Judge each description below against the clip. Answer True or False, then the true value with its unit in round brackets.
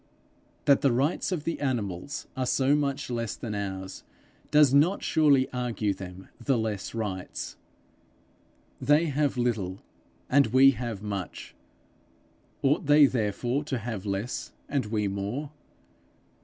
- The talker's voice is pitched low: True (125 Hz)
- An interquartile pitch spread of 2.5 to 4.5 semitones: False (5.4 semitones)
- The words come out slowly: True (130 wpm)